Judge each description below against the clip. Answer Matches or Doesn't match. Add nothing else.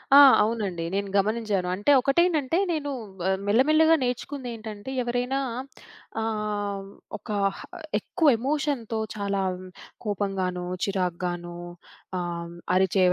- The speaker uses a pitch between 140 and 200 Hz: Doesn't match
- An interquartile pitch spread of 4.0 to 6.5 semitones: Matches